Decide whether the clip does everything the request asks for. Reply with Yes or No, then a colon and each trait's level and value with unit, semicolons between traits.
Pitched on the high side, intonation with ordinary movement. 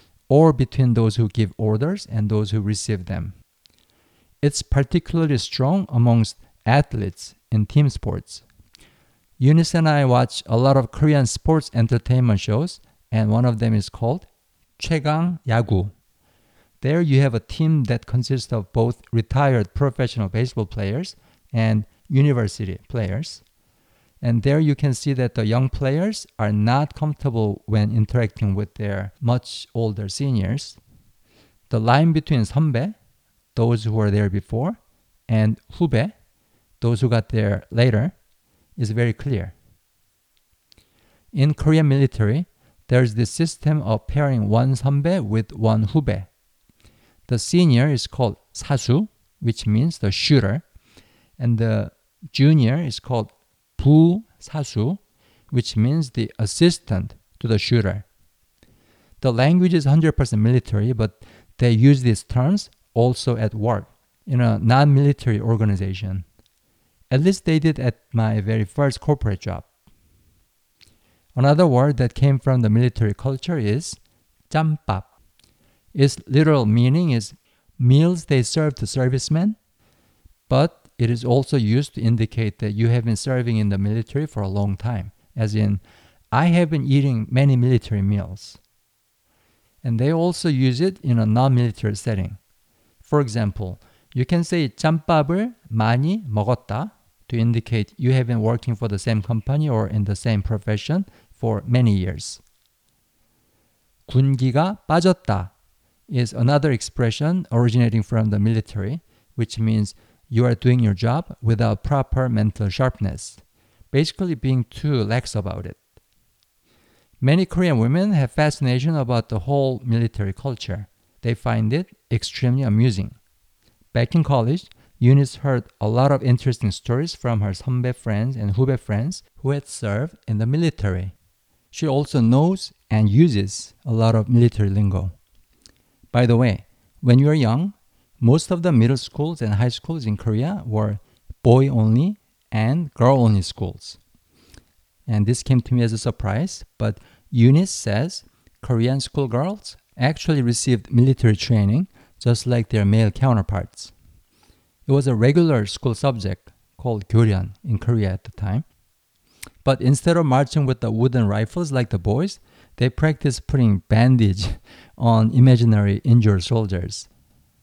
No: low, 120 Hz; average, 4.5 semitones